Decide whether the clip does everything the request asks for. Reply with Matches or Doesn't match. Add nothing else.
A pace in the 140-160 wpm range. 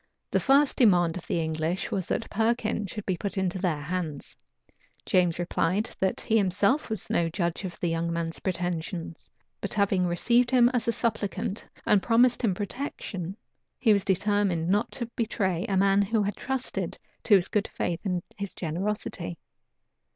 Doesn't match